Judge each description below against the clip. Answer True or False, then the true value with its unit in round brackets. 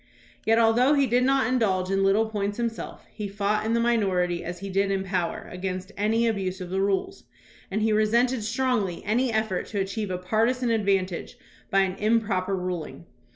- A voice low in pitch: False (205 Hz)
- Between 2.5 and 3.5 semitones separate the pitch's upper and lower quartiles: True (3.2 semitones)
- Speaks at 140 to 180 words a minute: False (190 wpm)